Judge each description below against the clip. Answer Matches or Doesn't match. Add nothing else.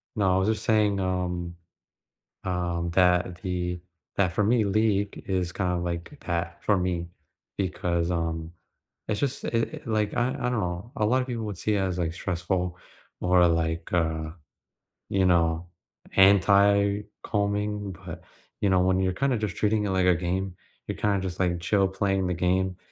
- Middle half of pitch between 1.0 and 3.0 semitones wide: Matches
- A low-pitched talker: Matches